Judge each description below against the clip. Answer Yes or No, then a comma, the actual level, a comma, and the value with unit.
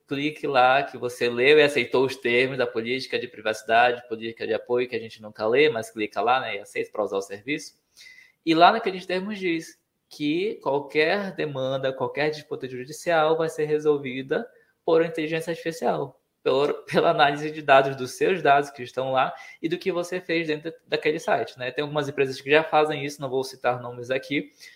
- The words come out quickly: Yes, fast, 190 wpm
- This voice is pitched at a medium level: Yes, medium, 150 Hz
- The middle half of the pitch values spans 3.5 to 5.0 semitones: Yes, average, 4.3 semitones